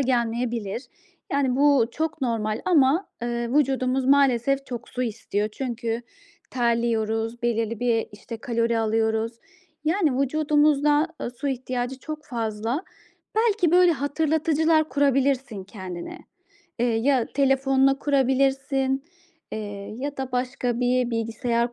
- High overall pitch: Yes, very high, 255 Hz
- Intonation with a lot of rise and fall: No, average, 3.3 semitones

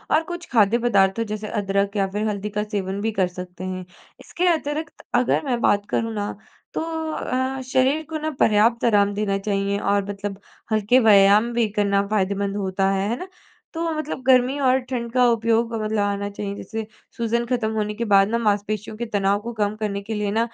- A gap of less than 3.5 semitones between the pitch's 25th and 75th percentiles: Yes, average, 2.8 semitones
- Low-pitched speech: No, high, 210 Hz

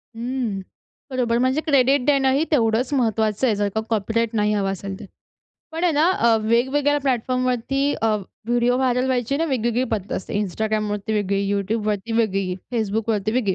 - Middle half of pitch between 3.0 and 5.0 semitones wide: Yes, average, 3.5 semitones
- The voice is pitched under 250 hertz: Yes, high, 230 Hz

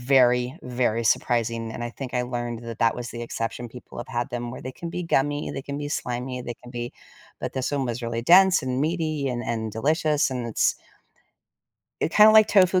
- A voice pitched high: No, low, 125 Hz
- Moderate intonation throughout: Yes, average, 3.5 semitones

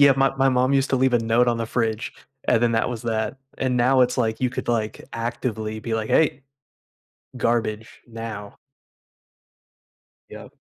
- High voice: No, low, 120 Hz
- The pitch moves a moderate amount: No, narrow, 2.3 semitones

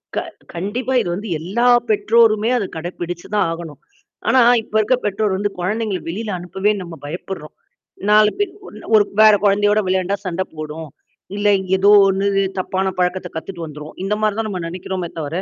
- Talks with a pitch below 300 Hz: Yes, high, 195 Hz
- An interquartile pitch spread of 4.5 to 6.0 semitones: No, average, 3.2 semitones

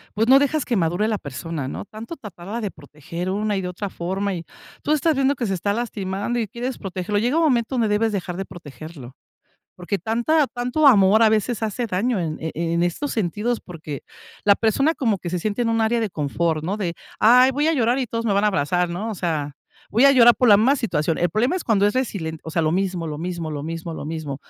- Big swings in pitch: Yes, wide, 5.7 semitones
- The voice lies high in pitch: Yes, high, 205 Hz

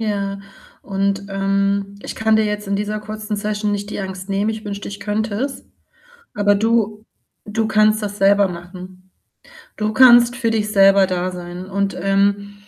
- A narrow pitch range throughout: Yes, narrow, 1.5 semitones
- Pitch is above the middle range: Yes, high, 205 Hz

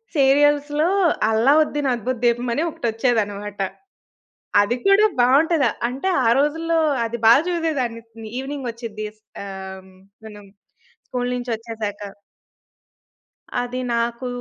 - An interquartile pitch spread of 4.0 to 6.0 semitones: Yes, average, 4.5 semitones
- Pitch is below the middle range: No, high, 245 Hz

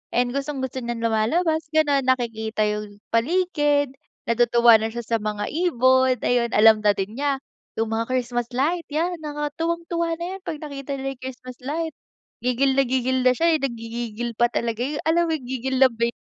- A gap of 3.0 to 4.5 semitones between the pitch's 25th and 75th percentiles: Yes, average, 4.0 semitones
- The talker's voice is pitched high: Yes, very high, 255 Hz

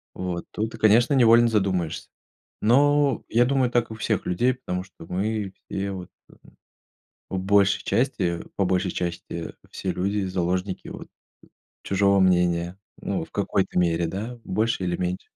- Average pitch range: Yes, average, 4.0 semitones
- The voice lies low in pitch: Yes, low, 100 Hz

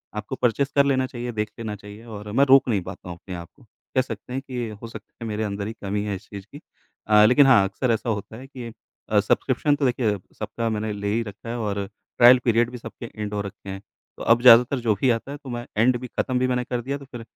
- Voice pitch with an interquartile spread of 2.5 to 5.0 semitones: Yes, average, 3.4 semitones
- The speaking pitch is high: No, low, 115 Hz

